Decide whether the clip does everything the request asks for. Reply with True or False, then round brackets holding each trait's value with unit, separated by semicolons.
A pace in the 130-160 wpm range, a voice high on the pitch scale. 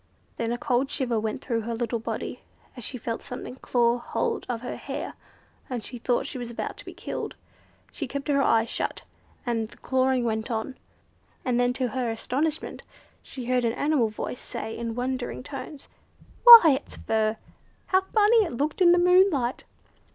False (180 wpm; 250 Hz)